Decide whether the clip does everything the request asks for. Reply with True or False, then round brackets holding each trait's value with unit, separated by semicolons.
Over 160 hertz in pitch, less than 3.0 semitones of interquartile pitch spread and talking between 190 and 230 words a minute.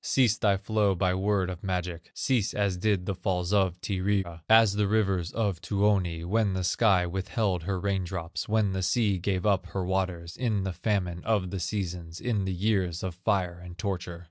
False (95 Hz; 2.4 semitones; 195 wpm)